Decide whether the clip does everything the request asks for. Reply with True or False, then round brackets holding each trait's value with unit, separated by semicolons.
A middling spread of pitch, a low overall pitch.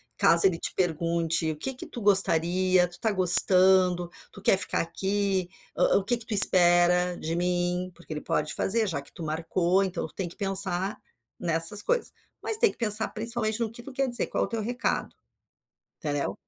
False (3.3 semitones; 185 Hz)